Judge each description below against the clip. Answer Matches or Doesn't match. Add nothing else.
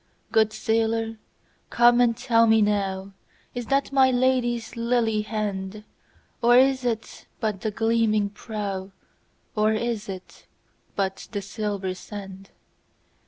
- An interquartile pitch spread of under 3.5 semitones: Matches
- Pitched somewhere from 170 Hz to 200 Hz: Doesn't match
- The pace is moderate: Doesn't match